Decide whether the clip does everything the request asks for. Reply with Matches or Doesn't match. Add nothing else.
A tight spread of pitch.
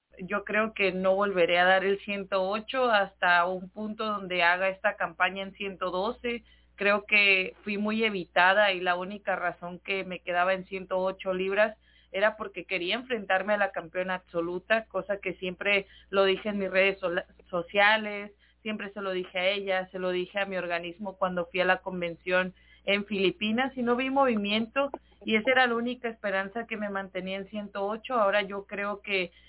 Matches